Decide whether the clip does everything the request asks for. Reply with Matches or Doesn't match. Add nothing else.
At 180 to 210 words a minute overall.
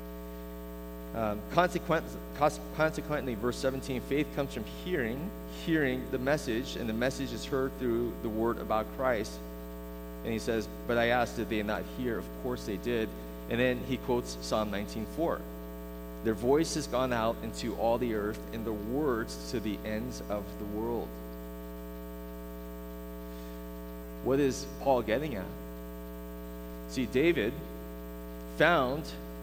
Doesn't match